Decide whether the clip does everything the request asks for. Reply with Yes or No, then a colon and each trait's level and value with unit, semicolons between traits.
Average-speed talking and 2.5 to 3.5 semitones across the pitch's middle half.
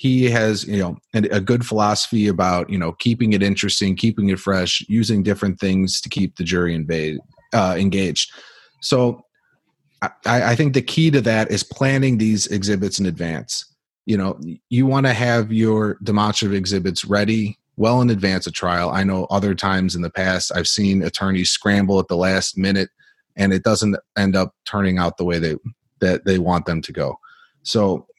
Yes: average, 185 wpm; average, 3.1 semitones